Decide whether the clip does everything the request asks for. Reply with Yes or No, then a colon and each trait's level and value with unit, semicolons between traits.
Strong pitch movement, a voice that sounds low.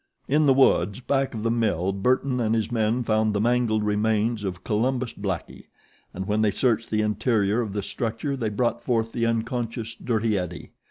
No: narrow, 2.4 semitones; low, 110 Hz